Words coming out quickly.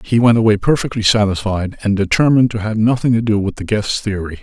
Yes: fast, 215 wpm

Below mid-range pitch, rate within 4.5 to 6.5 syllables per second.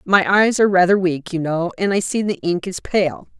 No: medium, 185 Hz; 5.0 syllables/s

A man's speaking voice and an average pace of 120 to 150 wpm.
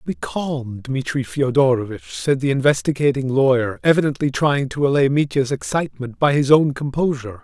Yes: male; average, 145 wpm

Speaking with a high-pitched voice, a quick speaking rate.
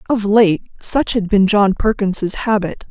No: high, 205 Hz; average, 165 wpm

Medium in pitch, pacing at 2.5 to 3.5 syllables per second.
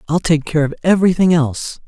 No: medium, 160 Hz; 6.4 syllables/s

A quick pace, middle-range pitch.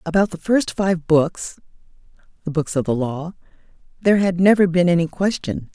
No: average, 145 wpm; medium, 175 Hz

